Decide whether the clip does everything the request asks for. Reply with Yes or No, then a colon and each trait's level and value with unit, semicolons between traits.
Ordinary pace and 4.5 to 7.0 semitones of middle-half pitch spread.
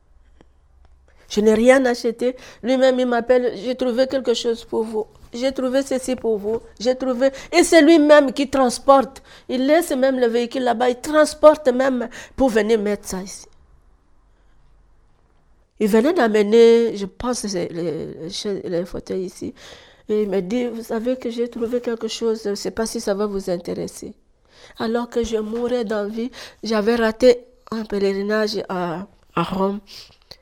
No: average, 160 wpm; average, 3.9 semitones